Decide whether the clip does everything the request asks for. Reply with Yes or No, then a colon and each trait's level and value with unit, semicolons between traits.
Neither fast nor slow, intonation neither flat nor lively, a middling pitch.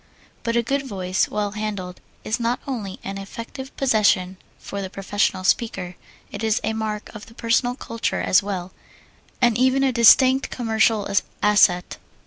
No: average, 150 wpm; average, 3.4 semitones; high, 215 Hz